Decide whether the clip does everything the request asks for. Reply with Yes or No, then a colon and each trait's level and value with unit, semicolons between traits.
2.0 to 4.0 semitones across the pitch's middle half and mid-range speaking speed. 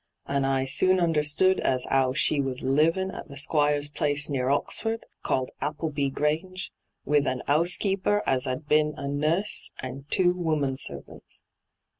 Yes: average, 3.6 semitones; average, 150 wpm